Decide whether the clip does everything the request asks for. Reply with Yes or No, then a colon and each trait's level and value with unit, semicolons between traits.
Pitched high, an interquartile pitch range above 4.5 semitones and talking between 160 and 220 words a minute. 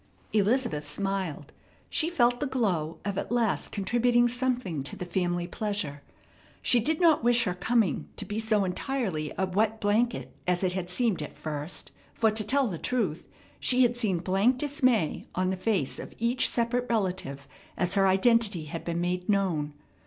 Yes: high, 205 Hz; average, 5.2 semitones; average, 175 wpm